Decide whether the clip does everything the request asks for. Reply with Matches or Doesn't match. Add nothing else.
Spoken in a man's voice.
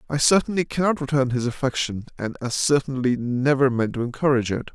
Matches